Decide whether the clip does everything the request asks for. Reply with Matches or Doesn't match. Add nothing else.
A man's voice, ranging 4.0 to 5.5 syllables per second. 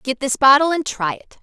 Doesn't match